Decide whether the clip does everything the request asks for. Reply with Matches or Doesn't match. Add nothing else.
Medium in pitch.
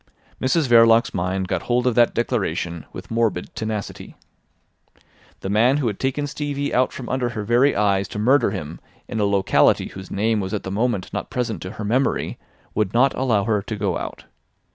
Doesn't match